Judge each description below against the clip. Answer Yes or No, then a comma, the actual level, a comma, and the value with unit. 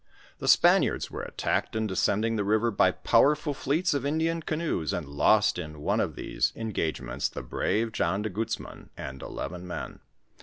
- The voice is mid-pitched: No, low, 110 Hz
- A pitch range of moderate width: No, wide, 8.2 semitones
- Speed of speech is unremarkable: Yes, average, 175 wpm